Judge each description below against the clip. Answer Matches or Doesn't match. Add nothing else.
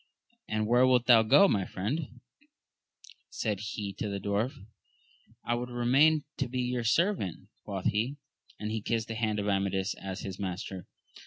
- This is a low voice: Matches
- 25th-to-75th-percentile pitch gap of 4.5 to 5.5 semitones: Doesn't match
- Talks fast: Doesn't match